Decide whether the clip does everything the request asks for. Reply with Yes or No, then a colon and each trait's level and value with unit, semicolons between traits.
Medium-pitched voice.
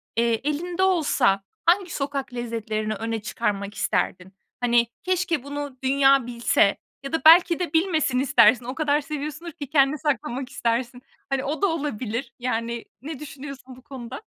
No: very high, 270 Hz